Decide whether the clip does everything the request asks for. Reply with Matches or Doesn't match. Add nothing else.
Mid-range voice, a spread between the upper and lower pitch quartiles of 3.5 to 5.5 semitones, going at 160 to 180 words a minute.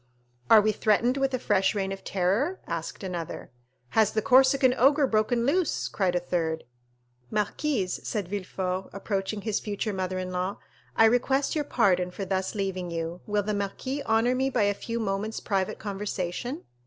Doesn't match